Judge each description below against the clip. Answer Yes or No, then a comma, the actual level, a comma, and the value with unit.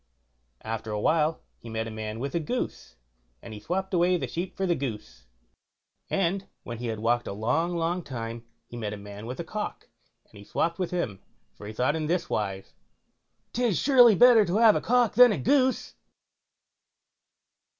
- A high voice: No, medium, 160 Hz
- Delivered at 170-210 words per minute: Yes, average, 190 wpm